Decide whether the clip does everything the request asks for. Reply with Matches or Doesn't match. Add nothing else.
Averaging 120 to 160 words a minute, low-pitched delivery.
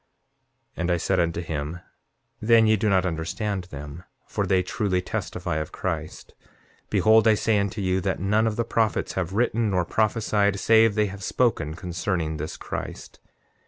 Doesn't match